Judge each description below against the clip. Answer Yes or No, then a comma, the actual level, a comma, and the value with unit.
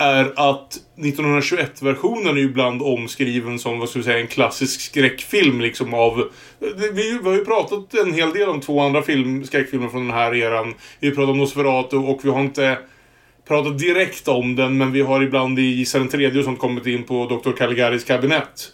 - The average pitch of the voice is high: No, low, 135 Hz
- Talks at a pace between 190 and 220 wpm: Yes, fast, 195 wpm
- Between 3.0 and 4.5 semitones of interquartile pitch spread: No, narrow, 2.5 semitones